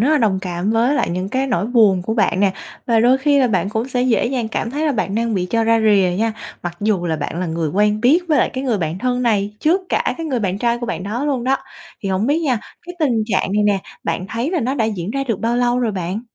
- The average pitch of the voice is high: Yes, high, 225 Hz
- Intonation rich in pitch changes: No, average, 4.6 semitones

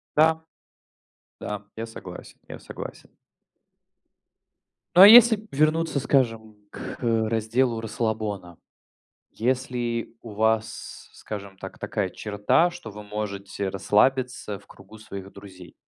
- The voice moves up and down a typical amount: Yes, average, 3.9 semitones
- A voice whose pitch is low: Yes, low, 110 Hz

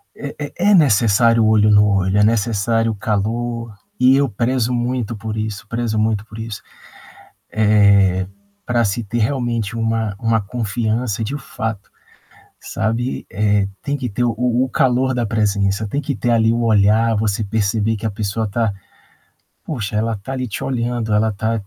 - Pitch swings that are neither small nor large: No, narrow, 2.3 semitones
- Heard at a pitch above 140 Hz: No, low, 110 Hz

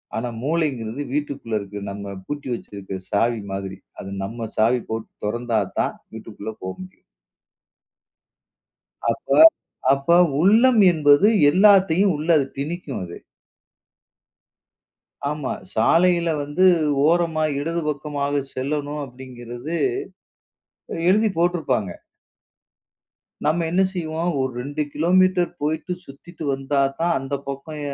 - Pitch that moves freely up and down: Yes, wide, 5.9 semitones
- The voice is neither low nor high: Yes, medium, 145 Hz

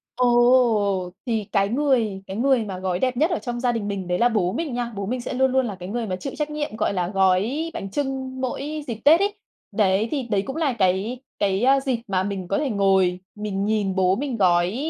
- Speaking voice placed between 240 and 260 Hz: No, high, 225 Hz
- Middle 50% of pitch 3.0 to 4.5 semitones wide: No, average, 5.2 semitones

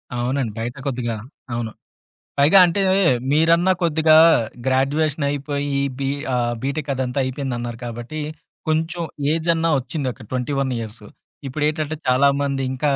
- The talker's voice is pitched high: No, medium, 140 Hz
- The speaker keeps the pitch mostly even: No, average, 3.7 semitones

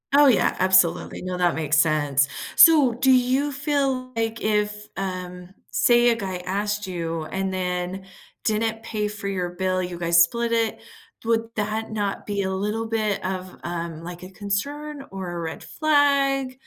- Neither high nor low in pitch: No, high, 205 Hz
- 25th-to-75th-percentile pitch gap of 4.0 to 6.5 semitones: Yes, average, 4.4 semitones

